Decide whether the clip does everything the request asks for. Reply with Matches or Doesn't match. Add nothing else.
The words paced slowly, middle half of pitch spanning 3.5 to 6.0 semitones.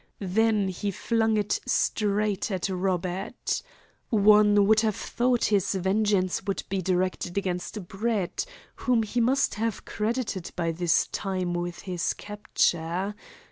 Doesn't match